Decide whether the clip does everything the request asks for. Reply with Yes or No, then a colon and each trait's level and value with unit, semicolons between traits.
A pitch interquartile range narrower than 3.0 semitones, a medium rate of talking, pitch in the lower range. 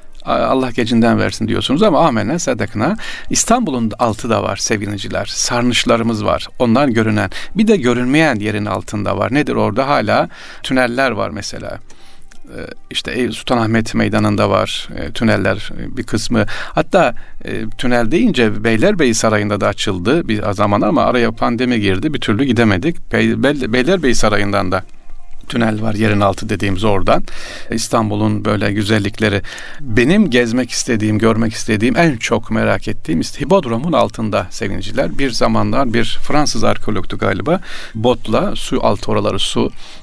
Yes: narrow, 2.6 semitones; average, 130 wpm; low, 110 Hz